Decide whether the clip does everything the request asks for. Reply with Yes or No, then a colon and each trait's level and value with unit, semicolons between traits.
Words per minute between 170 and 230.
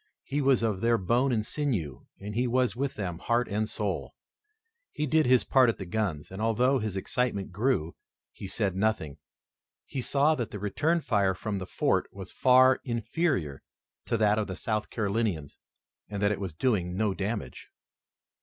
Yes: average, 180 wpm